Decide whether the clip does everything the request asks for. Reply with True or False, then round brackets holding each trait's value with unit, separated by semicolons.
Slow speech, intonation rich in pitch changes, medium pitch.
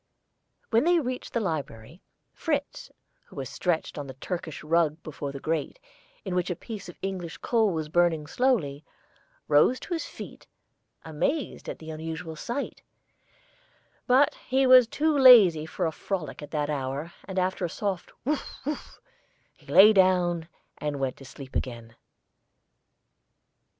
False (150 wpm; 7.1 semitones; 175 Hz)